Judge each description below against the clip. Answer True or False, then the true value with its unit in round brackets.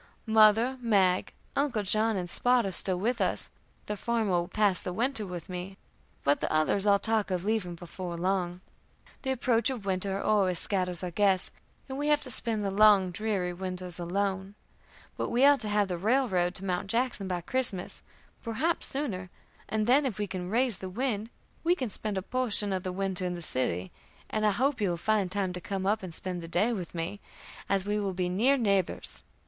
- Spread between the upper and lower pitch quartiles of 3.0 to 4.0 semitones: True (3.6 semitones)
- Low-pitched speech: False (200 Hz)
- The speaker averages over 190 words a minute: True (205 wpm)